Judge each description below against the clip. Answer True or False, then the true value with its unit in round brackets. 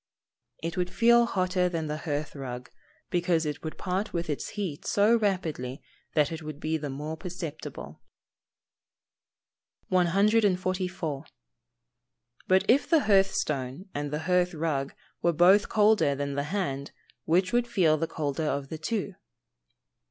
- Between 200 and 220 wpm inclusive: False (145 wpm)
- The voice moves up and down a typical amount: True (4.4 semitones)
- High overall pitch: False (170 Hz)